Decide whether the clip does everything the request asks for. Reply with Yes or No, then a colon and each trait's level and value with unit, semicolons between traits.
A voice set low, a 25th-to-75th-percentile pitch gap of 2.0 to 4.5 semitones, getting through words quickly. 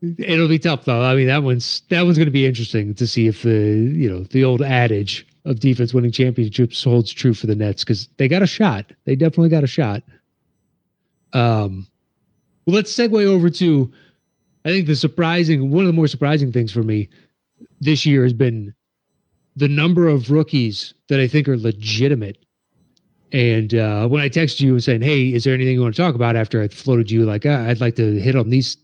No: low, 130 Hz; average, 4.9 semitones; fast, 210 wpm